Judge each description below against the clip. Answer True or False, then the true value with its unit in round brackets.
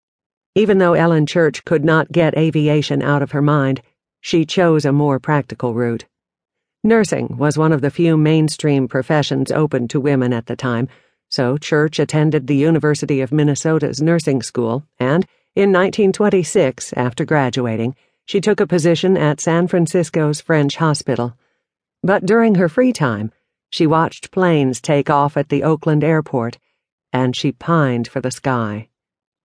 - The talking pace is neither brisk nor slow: True (155 wpm)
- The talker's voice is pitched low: False (150 Hz)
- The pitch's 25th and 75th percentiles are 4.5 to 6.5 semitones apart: False (3.8 semitones)